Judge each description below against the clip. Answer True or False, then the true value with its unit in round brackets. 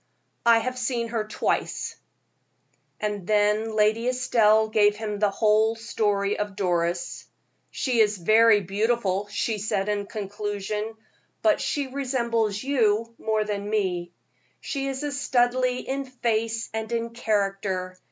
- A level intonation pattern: True (2.3 semitones)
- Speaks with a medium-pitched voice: False (215 Hz)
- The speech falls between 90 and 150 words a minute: True (135 wpm)